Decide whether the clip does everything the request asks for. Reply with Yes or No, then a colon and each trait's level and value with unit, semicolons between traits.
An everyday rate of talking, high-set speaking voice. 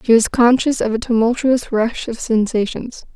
Yes: average, 170 wpm; high, 235 Hz